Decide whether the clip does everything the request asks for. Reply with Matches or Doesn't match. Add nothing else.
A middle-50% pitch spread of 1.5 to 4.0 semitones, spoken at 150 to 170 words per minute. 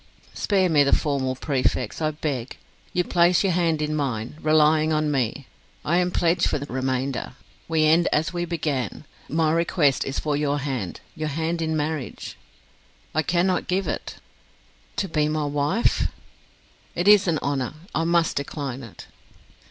Matches